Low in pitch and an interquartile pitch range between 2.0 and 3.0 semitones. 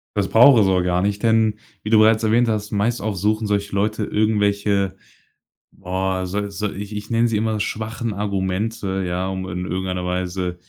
Yes: low, 100 Hz; narrow, 2.5 semitones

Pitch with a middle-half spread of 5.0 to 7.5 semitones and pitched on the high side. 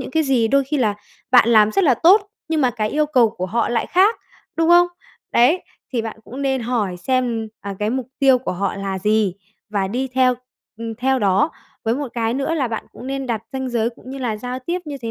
No: average, 3.5 semitones; very high, 250 Hz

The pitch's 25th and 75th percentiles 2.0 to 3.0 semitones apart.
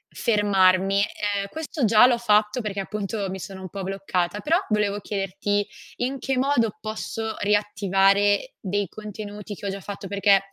No: narrow, 1.6 semitones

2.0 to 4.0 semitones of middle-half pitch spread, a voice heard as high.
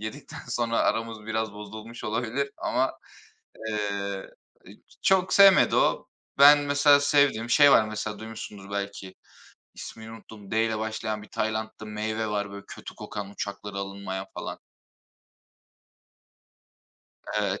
No: narrow, 2.4 semitones; low, 110 Hz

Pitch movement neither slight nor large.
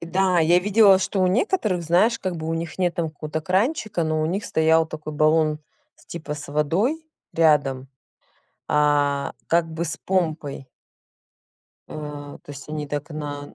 Yes: average, 3.4 semitones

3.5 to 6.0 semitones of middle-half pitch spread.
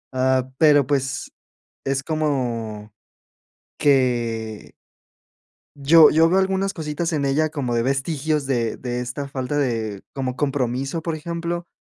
Yes: average, 3.9 semitones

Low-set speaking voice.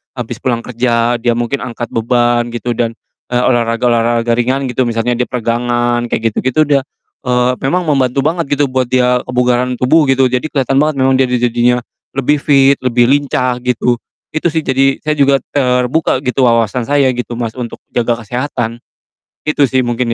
Yes: low, 125 Hz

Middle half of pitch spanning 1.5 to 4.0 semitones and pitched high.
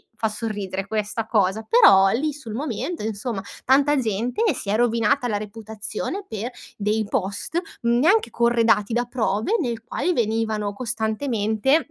Yes: average, 2.9 semitones; high, 225 Hz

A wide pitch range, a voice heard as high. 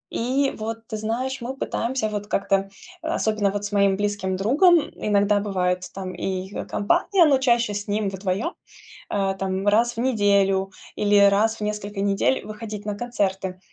No: average, 2.7 semitones; high, 205 Hz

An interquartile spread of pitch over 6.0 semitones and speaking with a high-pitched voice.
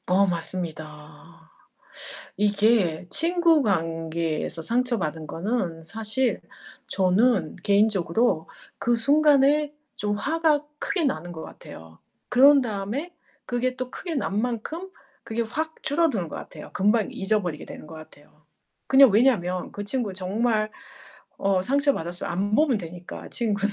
Yes: wide, 6.7 semitones; high, 210 Hz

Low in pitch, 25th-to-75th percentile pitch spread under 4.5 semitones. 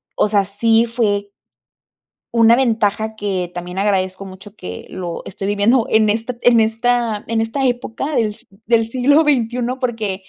No: high, 220 Hz; average, 2.8 semitones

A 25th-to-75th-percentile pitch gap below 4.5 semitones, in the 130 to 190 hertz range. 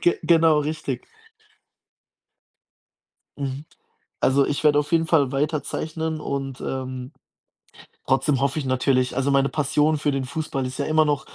Yes: narrow, 2.5 semitones; medium, 140 Hz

